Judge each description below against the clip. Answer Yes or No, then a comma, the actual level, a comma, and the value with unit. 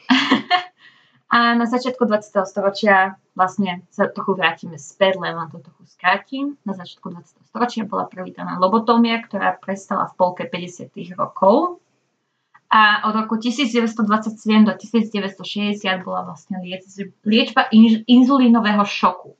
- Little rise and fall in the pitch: No, average, 3.9 semitones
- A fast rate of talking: No, average, 115 wpm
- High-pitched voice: Yes, high, 205 Hz